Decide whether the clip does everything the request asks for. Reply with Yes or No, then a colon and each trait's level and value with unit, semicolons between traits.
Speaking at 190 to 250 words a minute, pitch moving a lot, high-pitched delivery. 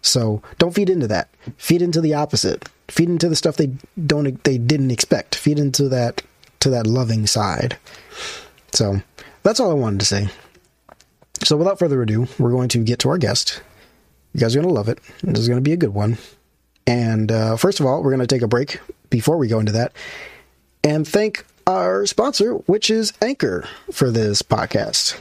No: average, 200 wpm; wide, 6.1 semitones; low, 130 Hz